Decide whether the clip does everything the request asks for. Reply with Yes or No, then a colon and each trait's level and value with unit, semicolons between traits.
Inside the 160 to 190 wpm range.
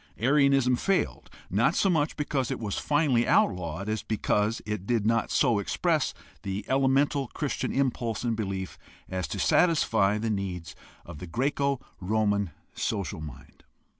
No: average, 145 wpm